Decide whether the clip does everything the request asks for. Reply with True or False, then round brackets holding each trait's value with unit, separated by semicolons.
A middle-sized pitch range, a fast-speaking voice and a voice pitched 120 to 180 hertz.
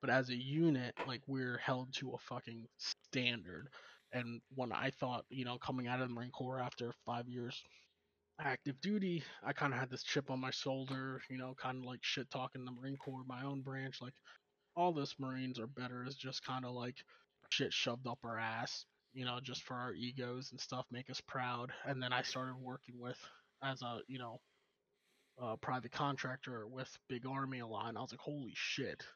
False (1.3 semitones; 210 wpm; 130 Hz)